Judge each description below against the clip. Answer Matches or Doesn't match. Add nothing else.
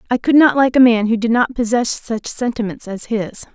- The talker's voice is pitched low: Doesn't match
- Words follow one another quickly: Matches